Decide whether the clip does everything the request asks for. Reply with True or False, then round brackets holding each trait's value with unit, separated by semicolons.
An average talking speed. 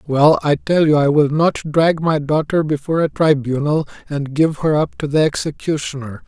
True (190 wpm)